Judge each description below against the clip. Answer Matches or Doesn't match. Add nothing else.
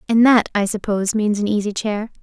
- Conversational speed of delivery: Doesn't match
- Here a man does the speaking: Doesn't match